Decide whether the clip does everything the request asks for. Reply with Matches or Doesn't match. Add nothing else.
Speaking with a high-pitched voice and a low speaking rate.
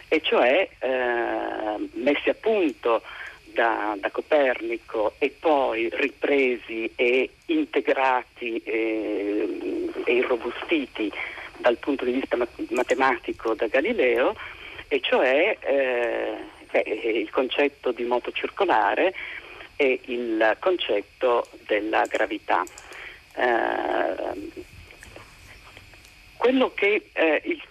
Matches